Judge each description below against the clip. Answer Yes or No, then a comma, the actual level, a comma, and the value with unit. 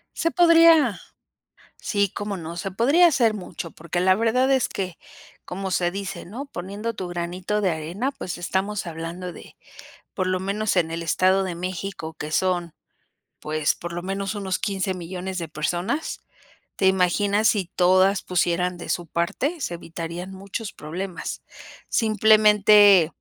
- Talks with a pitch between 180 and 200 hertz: Yes, high, 190 Hz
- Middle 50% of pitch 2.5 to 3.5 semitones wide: Yes, average, 3.2 semitones